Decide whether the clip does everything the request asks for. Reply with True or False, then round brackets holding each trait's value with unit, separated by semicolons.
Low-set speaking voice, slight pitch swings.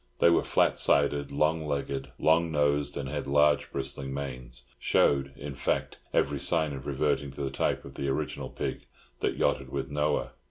True (70 Hz; 1.4 semitones)